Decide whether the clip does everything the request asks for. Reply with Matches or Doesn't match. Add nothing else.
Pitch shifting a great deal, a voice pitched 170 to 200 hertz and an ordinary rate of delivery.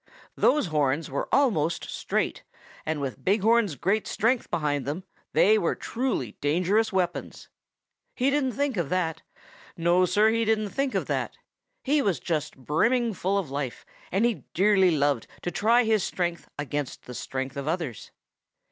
Matches